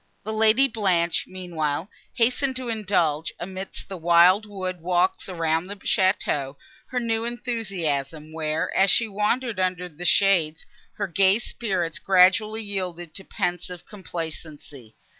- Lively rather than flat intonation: No, average, 4.2 semitones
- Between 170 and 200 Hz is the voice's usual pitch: Yes, medium, 185 Hz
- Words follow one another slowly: Yes, slow, 130 wpm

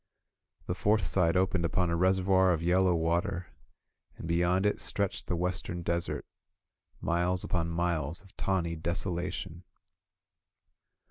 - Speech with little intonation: Yes, narrow, 1.8 semitones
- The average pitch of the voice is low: Yes, very low, 90 Hz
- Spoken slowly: Yes, slow, 130 wpm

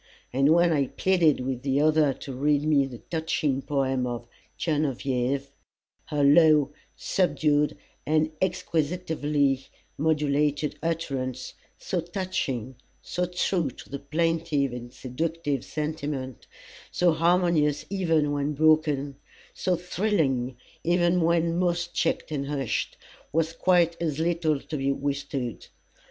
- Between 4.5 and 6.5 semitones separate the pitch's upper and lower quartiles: No, average, 3.3 semitones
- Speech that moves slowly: Yes, slow, 120 wpm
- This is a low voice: No, medium, 150 Hz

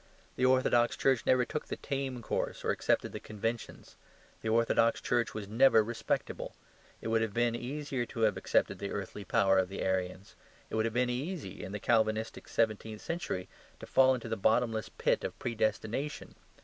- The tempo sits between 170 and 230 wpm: Yes, average, 180 wpm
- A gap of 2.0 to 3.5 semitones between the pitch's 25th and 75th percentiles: Yes, narrow, 2.6 semitones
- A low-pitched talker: Yes, low, 115 Hz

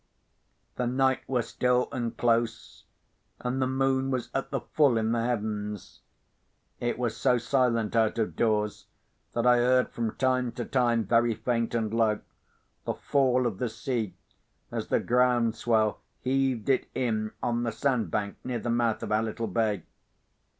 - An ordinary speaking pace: Yes, average, 165 wpm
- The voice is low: Yes, low, 120 Hz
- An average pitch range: No, narrow, 2.2 semitones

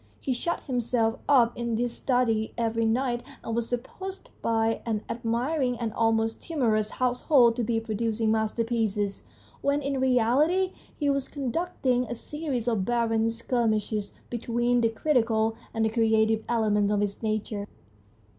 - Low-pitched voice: No, high, 230 Hz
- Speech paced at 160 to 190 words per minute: No, average, 145 wpm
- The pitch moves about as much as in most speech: No, narrow, 2.2 semitones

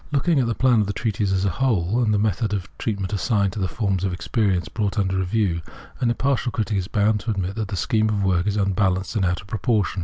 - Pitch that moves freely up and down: No, average, 2.8 semitones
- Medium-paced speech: No, fast, 265 wpm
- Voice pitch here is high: No, low, 100 Hz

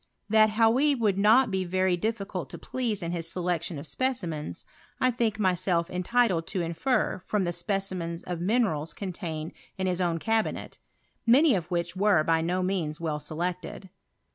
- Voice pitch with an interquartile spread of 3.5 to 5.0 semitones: Yes, average, 4.3 semitones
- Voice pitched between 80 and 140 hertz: No, medium, 185 Hz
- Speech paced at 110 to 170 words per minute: Yes, average, 165 wpm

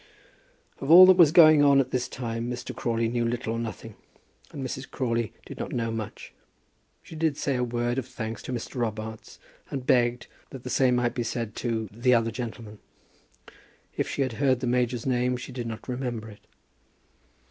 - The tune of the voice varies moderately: No, narrow, 2.1 semitones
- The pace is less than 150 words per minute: No, average, 190 wpm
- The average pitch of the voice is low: Yes, low, 120 Hz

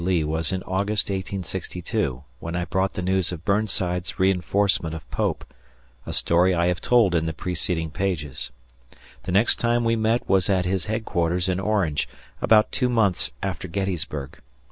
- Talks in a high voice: No, very low, 95 Hz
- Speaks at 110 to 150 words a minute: No, average, 165 wpm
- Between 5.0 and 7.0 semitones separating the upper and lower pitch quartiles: No, average, 2.7 semitones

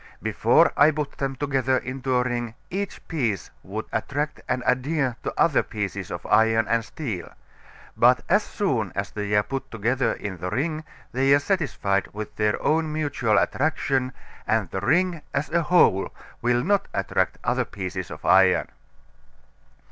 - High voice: No, low, 125 Hz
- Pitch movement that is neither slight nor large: No, wide, 6.1 semitones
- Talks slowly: No, average, 160 wpm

